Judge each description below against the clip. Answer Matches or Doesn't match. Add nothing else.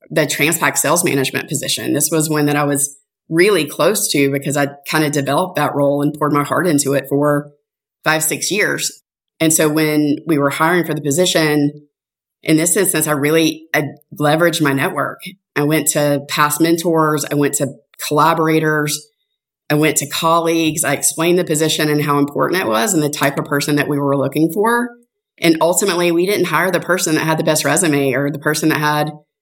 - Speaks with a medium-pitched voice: Matches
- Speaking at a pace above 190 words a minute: Matches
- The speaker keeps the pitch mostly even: Matches